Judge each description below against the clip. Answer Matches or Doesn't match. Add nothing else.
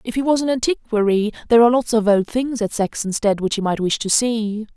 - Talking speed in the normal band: Doesn't match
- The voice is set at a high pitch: Matches